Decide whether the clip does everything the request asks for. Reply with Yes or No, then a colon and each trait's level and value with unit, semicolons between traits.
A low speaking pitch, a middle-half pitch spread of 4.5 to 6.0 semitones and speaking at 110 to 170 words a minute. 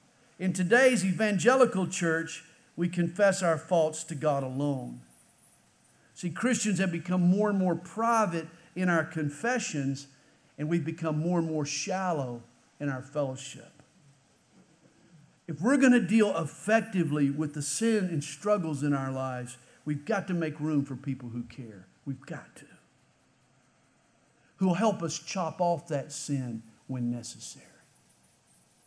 No: medium, 160 Hz; average, 4.8 semitones; average, 140 wpm